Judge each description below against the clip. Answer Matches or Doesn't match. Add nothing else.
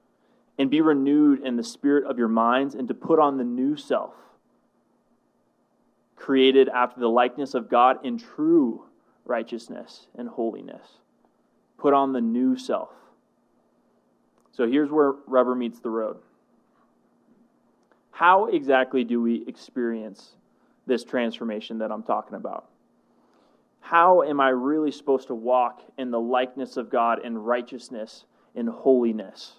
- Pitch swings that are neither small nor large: Matches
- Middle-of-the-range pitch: Doesn't match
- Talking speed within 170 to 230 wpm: Doesn't match